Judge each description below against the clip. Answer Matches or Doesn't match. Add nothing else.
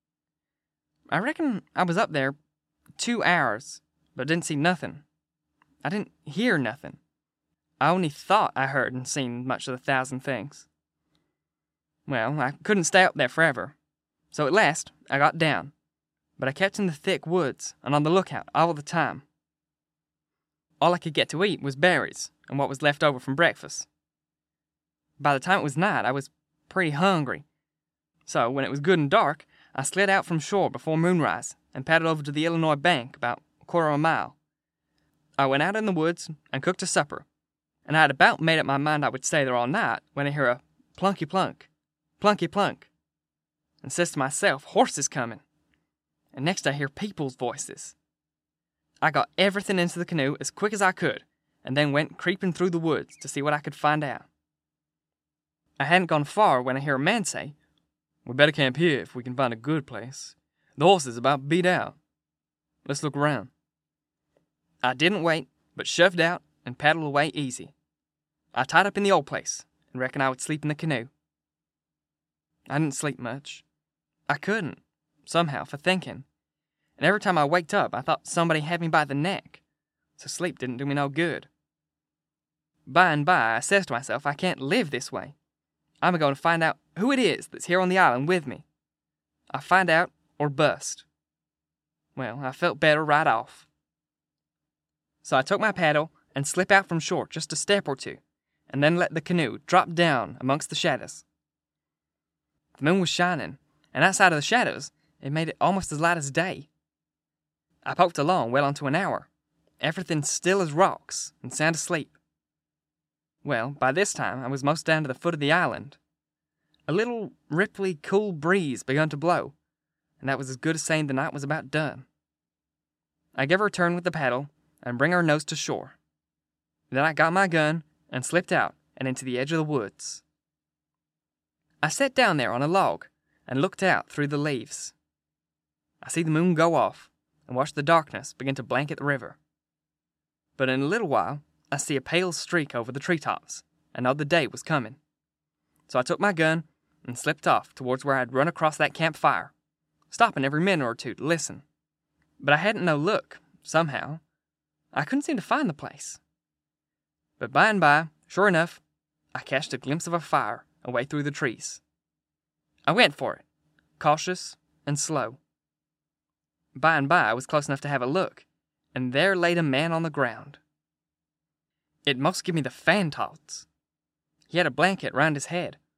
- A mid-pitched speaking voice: Matches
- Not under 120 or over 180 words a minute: Doesn't match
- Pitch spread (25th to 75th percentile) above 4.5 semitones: Doesn't match